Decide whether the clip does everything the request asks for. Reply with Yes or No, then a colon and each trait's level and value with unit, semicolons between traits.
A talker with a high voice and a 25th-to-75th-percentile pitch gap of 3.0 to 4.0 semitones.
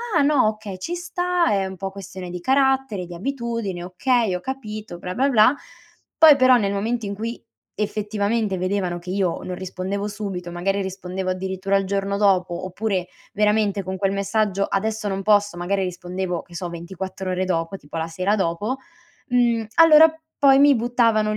Yes: high, 200 Hz; average, 3.5 semitones